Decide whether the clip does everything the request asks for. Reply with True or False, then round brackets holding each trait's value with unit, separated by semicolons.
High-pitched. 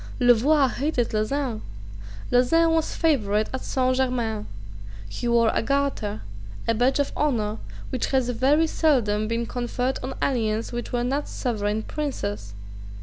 True (245 Hz)